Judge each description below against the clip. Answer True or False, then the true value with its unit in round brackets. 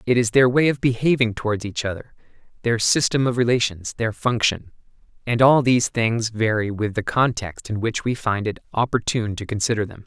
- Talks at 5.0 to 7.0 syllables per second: True (5.5 syllables/s)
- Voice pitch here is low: True (115 Hz)